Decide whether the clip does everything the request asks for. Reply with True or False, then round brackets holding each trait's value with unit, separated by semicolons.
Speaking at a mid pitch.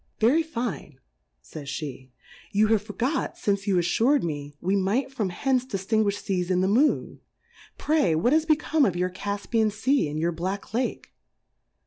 False (200 Hz)